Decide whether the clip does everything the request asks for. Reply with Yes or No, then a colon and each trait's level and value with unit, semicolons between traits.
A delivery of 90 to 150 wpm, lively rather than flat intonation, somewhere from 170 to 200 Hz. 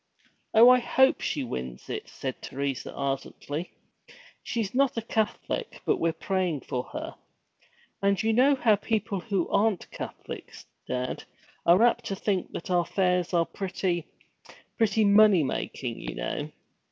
Yes: average, 145 wpm; wide, 6.8 semitones; high, 190 Hz